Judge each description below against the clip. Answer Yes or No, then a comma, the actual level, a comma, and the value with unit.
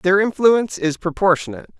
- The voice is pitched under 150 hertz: No, medium, 180 Hz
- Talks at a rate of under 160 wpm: Yes, slow, 135 wpm